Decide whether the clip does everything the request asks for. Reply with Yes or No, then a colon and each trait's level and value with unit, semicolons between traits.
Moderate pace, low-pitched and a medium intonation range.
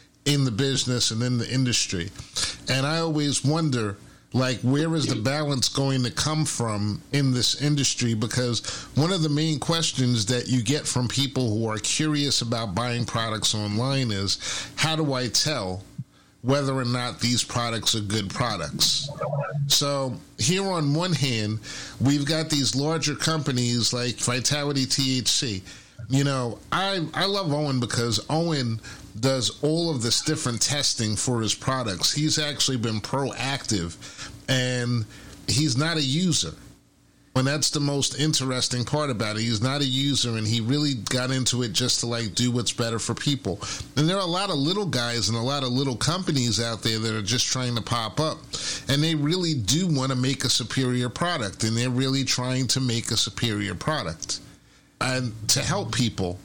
Yes: average, 175 wpm; low, 130 Hz; average, 3.7 semitones